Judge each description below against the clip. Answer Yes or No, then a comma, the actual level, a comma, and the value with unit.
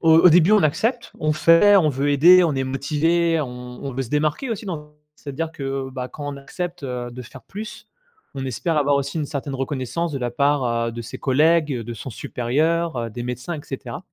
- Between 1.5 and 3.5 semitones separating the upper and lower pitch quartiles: No, average, 4.0 semitones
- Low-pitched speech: No, medium, 145 Hz